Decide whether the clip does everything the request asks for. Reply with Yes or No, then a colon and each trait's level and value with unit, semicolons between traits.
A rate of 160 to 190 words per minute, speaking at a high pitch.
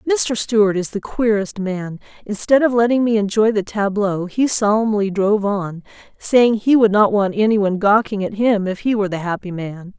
No: average, 200 wpm; high, 210 Hz